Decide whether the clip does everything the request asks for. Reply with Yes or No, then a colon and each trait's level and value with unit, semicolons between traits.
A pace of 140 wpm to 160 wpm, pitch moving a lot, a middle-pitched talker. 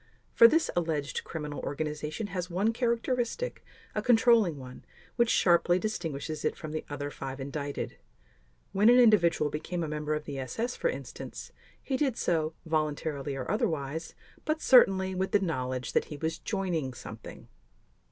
Yes: average, 155 wpm; wide, 6.8 semitones; medium, 165 Hz